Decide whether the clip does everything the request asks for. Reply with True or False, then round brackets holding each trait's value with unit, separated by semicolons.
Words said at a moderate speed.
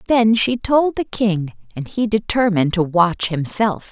True (170 wpm)